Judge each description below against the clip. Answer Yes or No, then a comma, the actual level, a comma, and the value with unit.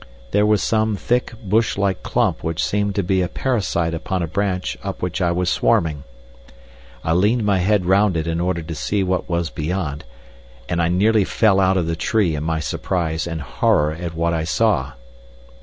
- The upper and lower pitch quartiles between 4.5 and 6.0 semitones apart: No, average, 3.6 semitones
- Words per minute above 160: Yes, average, 195 wpm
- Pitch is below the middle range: Yes, very low, 90 Hz